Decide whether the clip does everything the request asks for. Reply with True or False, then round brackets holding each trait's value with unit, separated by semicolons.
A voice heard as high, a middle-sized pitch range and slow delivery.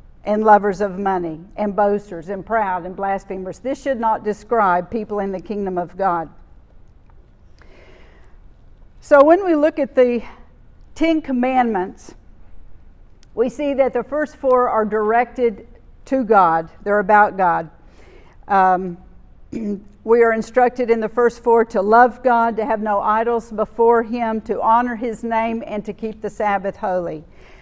False (215 Hz; 3.6 semitones; 150 wpm)